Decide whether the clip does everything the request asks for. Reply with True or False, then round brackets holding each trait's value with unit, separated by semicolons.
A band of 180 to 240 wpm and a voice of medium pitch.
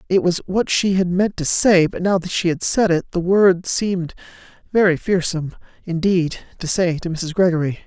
True (190 wpm; 180 Hz)